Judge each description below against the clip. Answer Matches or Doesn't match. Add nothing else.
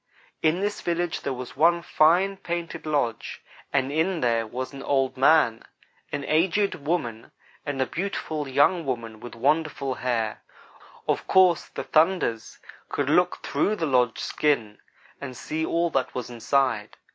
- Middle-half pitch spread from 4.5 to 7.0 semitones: Matches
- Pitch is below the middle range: Doesn't match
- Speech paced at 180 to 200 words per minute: Doesn't match